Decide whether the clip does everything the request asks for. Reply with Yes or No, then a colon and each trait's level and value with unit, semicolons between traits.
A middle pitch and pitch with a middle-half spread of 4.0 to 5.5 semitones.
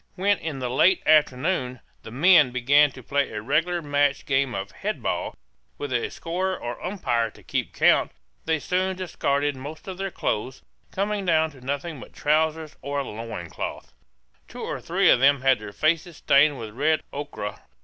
Yes: medium, 145 Hz; average, 4.4 semitones